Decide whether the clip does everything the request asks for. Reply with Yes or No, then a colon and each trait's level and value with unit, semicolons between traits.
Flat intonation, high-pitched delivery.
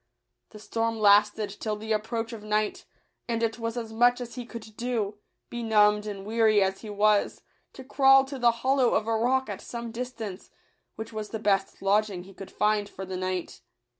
Yes: narrow, 2.1 semitones; high, 220 Hz